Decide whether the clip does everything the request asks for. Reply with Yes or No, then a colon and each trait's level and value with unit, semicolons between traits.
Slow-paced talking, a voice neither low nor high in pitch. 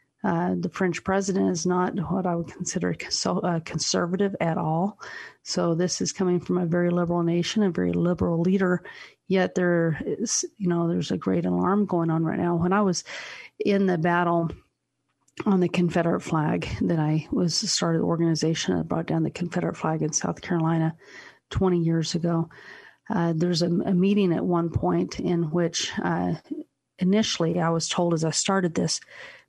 No: average, 180 wpm; medium, 175 Hz